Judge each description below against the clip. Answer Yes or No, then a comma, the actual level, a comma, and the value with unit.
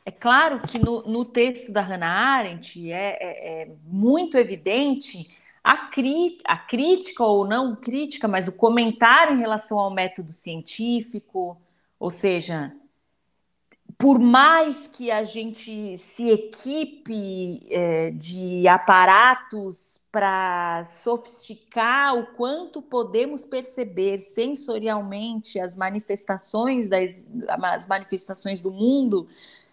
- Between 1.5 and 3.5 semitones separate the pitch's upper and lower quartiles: No, average, 4.7 semitones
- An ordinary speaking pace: No, slow, 110 wpm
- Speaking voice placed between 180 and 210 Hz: No, high, 220 Hz